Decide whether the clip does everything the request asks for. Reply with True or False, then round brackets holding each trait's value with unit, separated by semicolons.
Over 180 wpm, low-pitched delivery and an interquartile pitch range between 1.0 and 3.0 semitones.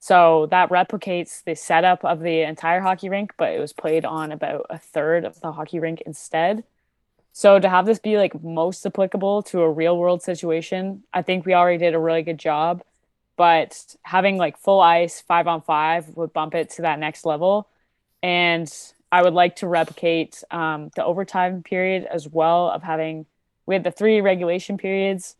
False (190 wpm; 175 Hz; 2.5 semitones)